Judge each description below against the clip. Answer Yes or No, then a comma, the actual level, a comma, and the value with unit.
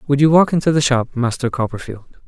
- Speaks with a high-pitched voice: No, low, 135 Hz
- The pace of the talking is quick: Yes, fast, 210 wpm